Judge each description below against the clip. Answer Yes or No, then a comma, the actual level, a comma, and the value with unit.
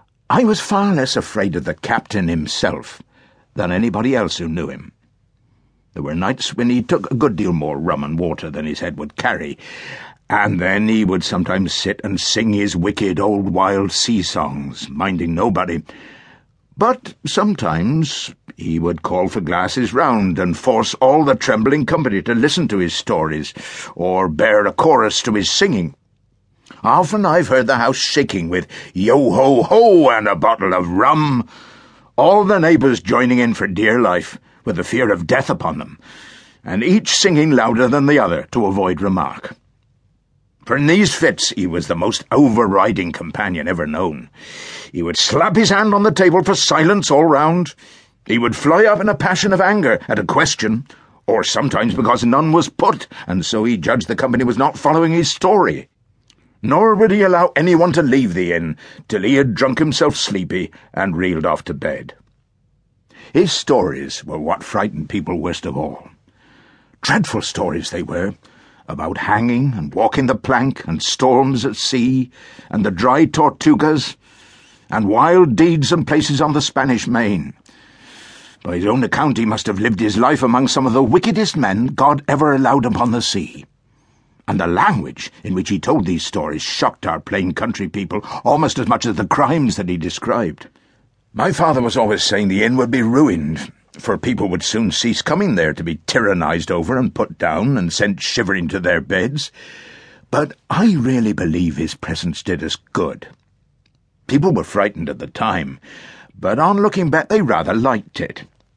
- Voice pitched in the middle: No, low, 130 Hz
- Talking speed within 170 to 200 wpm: Yes, average, 180 wpm